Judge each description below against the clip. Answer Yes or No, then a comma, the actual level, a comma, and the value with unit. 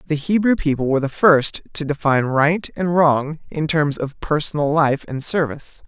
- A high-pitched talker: No, medium, 150 Hz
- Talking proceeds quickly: No, average, 185 wpm